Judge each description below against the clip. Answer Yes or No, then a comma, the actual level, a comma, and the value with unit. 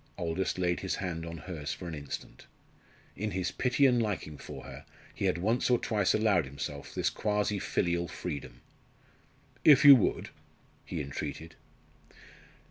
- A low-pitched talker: Yes, very low, 90 Hz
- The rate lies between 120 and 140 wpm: No, average, 150 wpm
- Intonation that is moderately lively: Yes, average, 4.4 semitones